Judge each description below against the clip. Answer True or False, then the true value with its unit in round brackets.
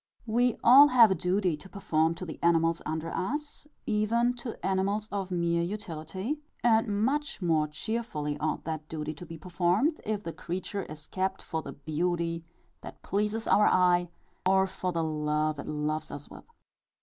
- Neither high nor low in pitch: True (180 Hz)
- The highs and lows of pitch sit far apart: False (4.9 semitones)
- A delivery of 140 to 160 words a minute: False (170 wpm)